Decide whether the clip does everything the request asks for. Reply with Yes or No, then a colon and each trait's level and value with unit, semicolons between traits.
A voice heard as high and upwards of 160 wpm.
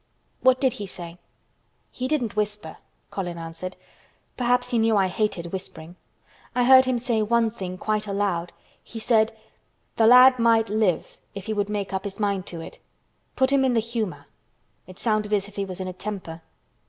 Yes: high, 210 Hz; average, 185 wpm